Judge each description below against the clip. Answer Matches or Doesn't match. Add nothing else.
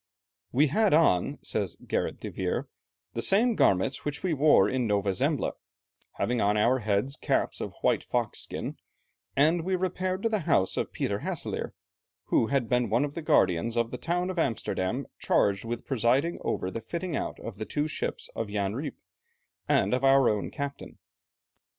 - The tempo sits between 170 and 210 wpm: Matches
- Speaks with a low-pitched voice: Matches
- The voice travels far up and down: Matches